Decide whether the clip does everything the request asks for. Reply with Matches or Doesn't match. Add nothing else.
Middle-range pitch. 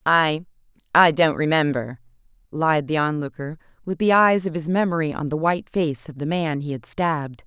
Matches